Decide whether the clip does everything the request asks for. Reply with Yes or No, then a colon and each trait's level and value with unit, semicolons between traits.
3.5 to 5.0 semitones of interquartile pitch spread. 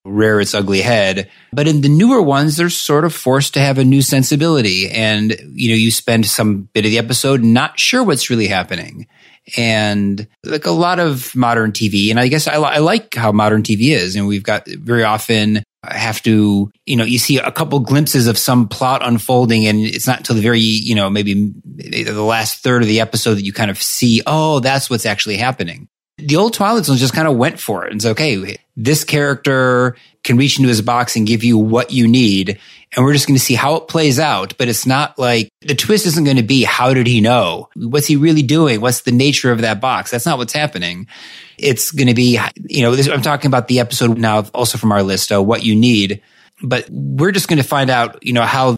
Yes: average, 4.5 semitones